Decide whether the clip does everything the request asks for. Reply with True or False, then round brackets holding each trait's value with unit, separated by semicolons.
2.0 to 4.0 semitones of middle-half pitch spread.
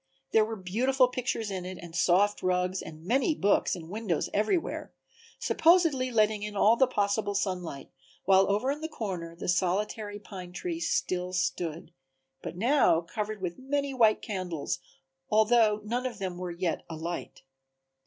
False (4.5 semitones)